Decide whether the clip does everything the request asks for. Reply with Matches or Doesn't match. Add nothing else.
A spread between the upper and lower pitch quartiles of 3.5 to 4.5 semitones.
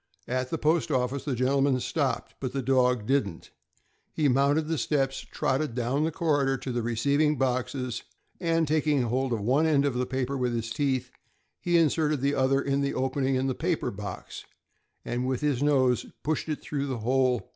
Doesn't match